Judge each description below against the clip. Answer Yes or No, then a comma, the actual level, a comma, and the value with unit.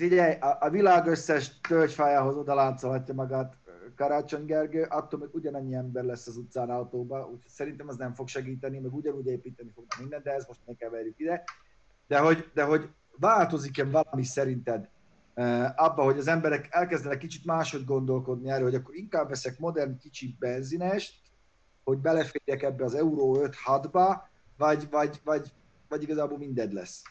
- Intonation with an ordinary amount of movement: Yes, average, 3.1 semitones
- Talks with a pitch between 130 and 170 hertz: Yes, medium, 140 Hz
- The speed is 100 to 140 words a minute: No, fast, 155 wpm